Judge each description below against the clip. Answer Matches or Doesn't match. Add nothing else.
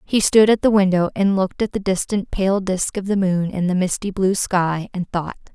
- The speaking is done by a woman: Matches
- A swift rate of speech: Matches